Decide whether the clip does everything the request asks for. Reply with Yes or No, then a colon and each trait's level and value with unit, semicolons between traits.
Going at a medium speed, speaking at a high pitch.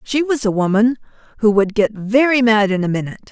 No: fast, 215 wpm; high, 220 Hz